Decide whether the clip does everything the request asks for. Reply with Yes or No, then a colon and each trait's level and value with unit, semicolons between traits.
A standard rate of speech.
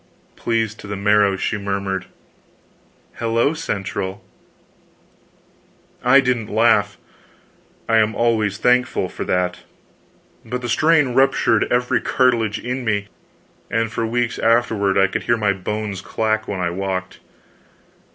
No: slow, 125 wpm